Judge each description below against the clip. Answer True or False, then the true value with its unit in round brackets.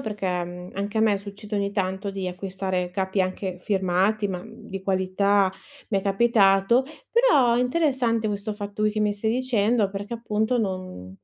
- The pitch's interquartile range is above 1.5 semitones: True (2.4 semitones)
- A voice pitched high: True (200 Hz)